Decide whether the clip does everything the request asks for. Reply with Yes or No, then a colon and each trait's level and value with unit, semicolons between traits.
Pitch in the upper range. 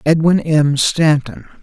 No: medium, 150 Hz